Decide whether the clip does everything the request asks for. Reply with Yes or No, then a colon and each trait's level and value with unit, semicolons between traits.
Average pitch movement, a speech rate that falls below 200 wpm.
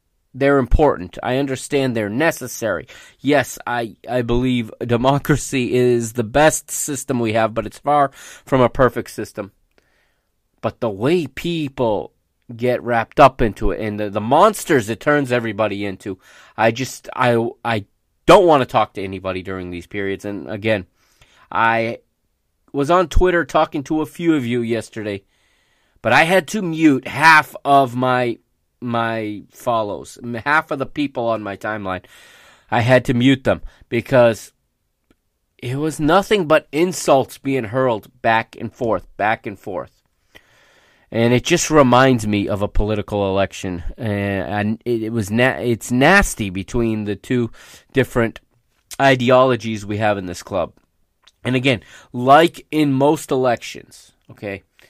Yes: average, 4.2 semitones; average, 145 wpm